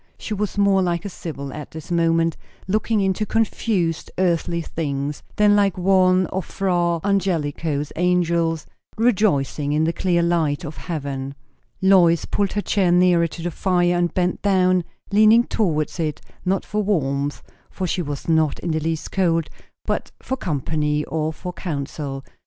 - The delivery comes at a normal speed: Yes, average, 160 wpm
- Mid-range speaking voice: Yes, medium, 170 Hz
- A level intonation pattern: No, average, 3.5 semitones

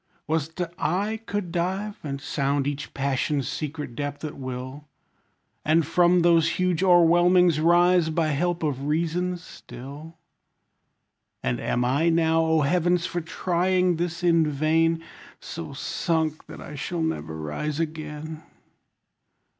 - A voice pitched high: No, medium, 160 Hz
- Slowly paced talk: Yes, slow, 130 wpm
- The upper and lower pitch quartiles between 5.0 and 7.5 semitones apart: No, average, 3.1 semitones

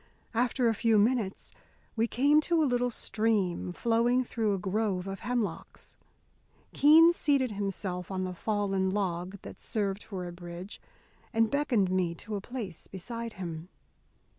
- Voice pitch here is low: No, high, 210 Hz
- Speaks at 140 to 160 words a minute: Yes, average, 150 wpm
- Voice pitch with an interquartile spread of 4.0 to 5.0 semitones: Yes, average, 4.3 semitones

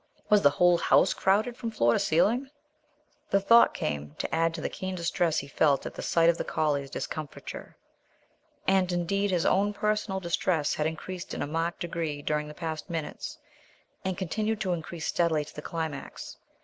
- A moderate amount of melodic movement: Yes, average, 3.7 semitones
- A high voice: No, medium, 170 Hz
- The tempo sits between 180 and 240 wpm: Yes, average, 185 wpm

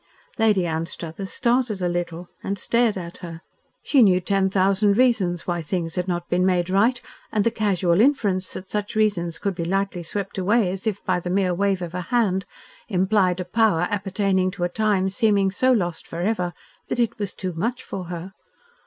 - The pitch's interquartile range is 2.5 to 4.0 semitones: Yes, average, 2.9 semitones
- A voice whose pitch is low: No, high, 190 Hz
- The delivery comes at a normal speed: Yes, average, 190 wpm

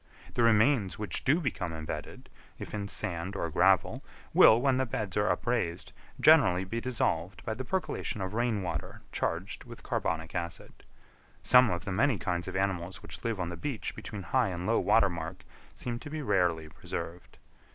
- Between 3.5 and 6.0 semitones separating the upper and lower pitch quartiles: Yes, average, 5.2 semitones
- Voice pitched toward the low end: Yes, low, 100 Hz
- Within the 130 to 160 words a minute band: No, average, 180 wpm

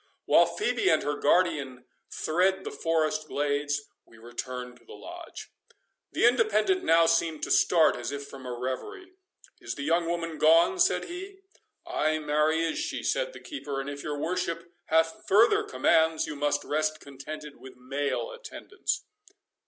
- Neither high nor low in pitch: Yes, medium, 155 Hz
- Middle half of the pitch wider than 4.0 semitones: Yes, average, 4.6 semitones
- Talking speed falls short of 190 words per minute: Yes, average, 160 wpm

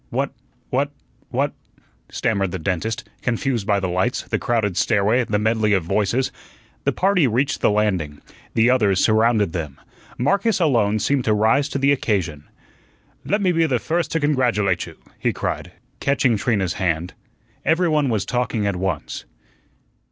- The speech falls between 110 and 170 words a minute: Yes, average, 160 wpm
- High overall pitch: No, low, 110 Hz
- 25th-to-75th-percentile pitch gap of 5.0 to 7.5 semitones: Yes, wide, 5.5 semitones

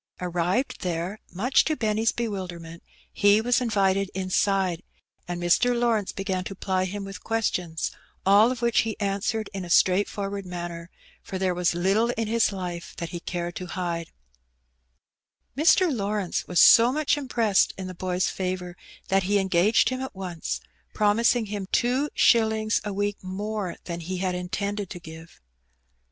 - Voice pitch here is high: Yes, high, 195 Hz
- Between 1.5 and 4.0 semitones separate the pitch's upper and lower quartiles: Yes, average, 3.4 semitones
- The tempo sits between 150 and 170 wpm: Yes, average, 160 wpm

